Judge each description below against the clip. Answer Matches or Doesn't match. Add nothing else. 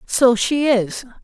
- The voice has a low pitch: Doesn't match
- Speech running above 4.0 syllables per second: Doesn't match